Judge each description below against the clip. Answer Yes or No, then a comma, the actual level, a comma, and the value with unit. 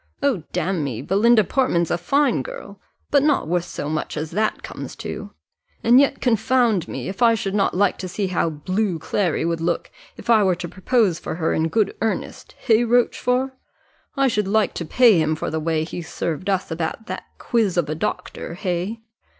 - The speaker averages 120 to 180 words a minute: No, average, 195 wpm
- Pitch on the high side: Yes, high, 195 Hz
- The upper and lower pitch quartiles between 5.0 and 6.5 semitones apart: Yes, wide, 5.6 semitones